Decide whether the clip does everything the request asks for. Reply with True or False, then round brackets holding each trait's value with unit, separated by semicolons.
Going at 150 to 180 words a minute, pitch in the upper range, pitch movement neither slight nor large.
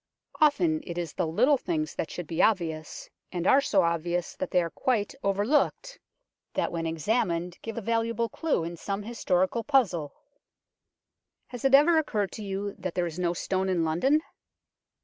False (170 wpm; 195 Hz; 6.4 semitones)